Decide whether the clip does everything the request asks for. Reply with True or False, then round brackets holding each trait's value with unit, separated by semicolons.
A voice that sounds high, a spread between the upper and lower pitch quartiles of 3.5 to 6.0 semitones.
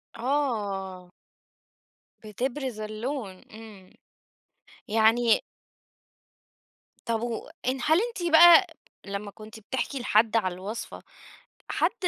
True (225 Hz; 4.1 semitones)